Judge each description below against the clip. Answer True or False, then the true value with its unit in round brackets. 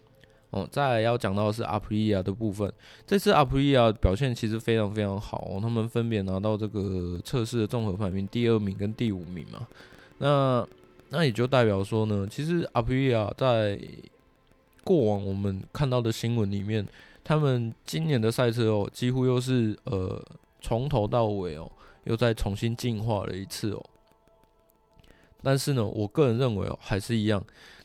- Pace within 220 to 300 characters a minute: True (260 characters per minute)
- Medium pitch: False (110 Hz)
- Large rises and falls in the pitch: False (3.3 semitones)